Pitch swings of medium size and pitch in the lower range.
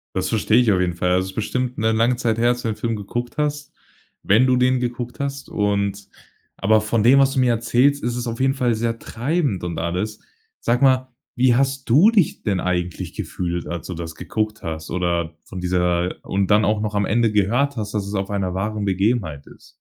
Yes: average, 4.6 semitones; low, 110 Hz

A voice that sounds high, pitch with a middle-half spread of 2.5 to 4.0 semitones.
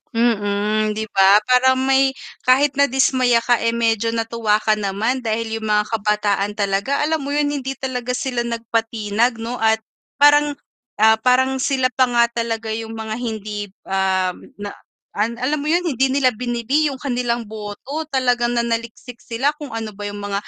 Yes: high, 235 Hz; average, 3.3 semitones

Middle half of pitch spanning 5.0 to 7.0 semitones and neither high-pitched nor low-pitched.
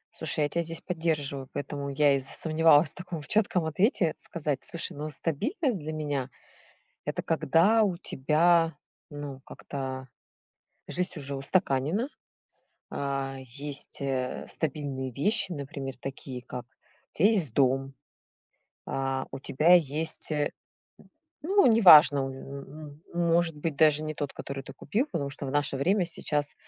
No: average, 3.5 semitones; medium, 150 Hz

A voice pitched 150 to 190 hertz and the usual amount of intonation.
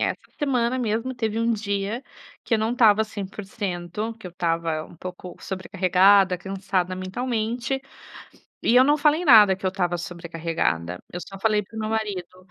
No: high, 200 Hz; average, 3.9 semitones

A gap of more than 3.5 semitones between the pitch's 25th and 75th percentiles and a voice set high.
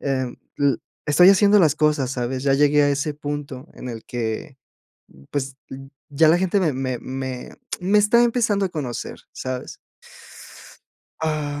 No: average, 4.4 semitones; medium, 145 Hz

